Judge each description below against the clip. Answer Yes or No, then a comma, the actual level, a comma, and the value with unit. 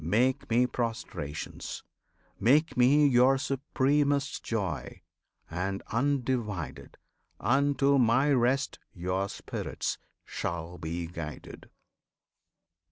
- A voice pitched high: No, low, 120 Hz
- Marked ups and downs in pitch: Yes, wide, 7.0 semitones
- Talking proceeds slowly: Yes, slow, 85 wpm